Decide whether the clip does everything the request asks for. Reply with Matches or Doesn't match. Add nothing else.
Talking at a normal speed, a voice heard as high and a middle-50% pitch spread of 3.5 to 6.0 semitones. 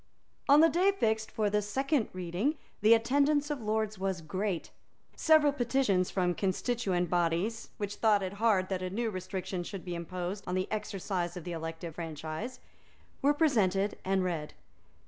Matches